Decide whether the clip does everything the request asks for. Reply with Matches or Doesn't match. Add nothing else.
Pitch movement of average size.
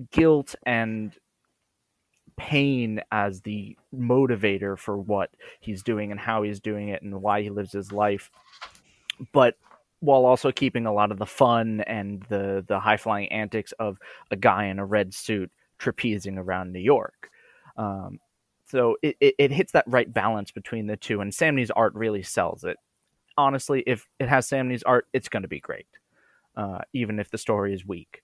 Matches